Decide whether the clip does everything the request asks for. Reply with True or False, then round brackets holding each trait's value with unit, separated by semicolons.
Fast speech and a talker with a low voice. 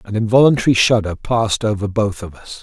False (185 wpm; 110 Hz)